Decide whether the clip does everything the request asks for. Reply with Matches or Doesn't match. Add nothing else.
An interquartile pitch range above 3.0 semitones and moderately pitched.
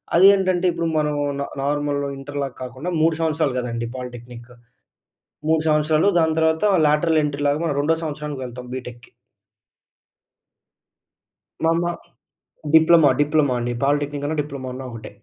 Matches